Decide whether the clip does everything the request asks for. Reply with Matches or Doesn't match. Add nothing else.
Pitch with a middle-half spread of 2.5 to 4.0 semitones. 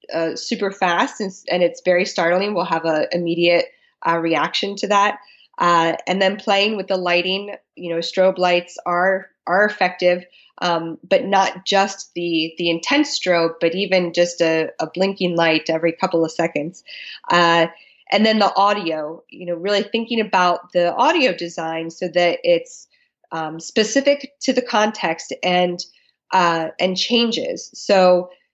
Matches